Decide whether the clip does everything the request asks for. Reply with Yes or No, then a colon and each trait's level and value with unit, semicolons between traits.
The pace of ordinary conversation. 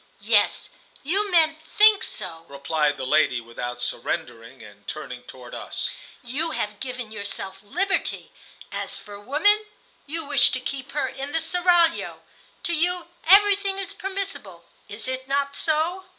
Yes: average, 145 wpm